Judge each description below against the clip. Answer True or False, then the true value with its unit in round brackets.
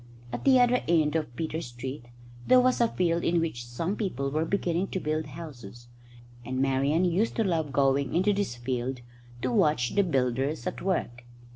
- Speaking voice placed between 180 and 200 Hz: False (155 Hz)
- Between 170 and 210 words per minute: True (180 wpm)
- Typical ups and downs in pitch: False (5.8 semitones)